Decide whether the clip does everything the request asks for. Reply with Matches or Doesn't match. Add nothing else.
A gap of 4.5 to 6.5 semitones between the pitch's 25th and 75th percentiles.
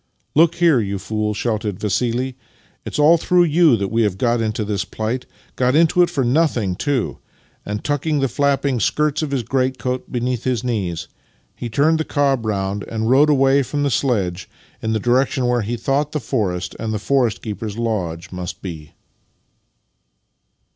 Matches